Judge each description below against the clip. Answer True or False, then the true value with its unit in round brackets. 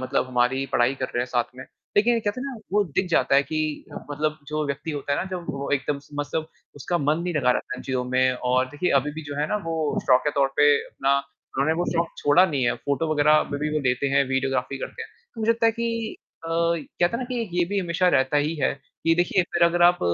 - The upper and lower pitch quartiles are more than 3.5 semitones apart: True (4.3 semitones)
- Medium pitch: True (150 Hz)